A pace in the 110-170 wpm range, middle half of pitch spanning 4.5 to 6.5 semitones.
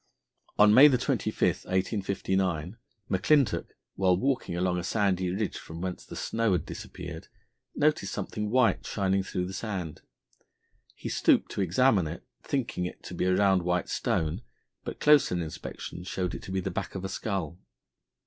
No: average, 160 wpm; average, 2.9 semitones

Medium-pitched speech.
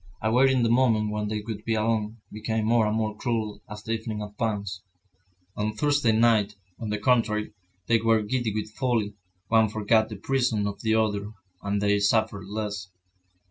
No: low, 110 Hz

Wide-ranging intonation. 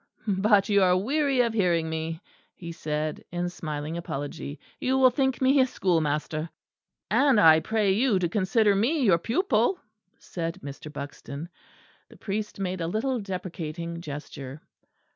Yes: wide, 5.7 semitones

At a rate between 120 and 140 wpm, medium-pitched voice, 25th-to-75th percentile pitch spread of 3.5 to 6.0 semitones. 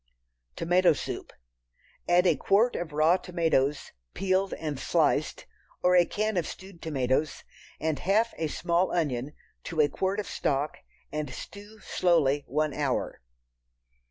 Yes: slow, 135 wpm; medium, 165 Hz; average, 4.1 semitones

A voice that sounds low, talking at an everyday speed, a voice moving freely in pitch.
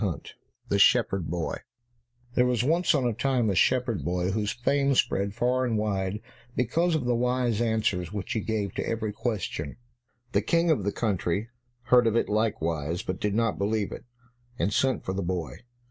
No: low, 110 Hz; average, 185 wpm; average, 4.1 semitones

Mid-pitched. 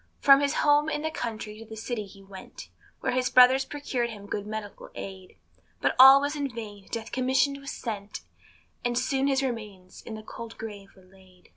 No: high, 230 Hz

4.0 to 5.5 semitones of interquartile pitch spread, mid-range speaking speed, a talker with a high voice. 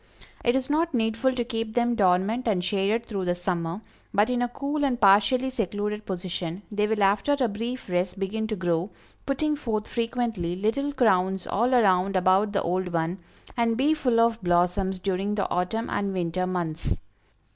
Yes: average, 4.5 semitones; average, 180 wpm; high, 210 Hz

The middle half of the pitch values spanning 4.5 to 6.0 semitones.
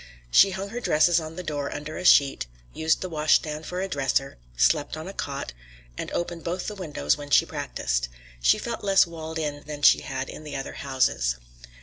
No: average, 3.8 semitones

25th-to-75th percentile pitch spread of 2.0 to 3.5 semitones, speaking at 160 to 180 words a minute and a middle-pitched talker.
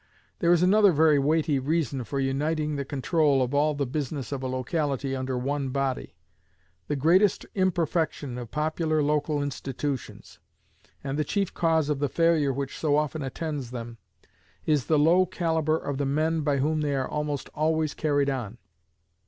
Yes: narrow, 2.6 semitones; average, 170 wpm; medium, 145 Hz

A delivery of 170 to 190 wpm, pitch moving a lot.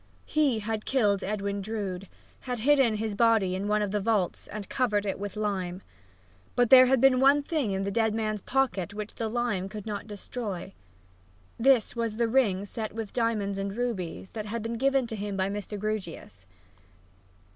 No: average, 185 wpm; average, 2.8 semitones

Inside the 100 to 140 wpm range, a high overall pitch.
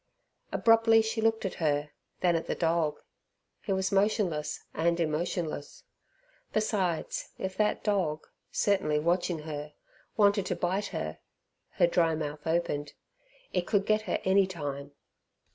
No: slow, 135 wpm; medium, 175 Hz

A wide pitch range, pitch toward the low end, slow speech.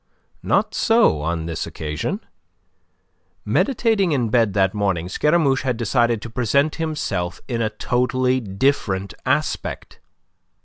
Yes: wide, 6.4 semitones; low, 120 Hz; slow, 120 wpm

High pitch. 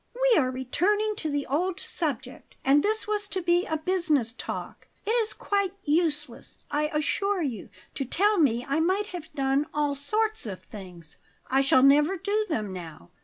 Yes: very high, 305 Hz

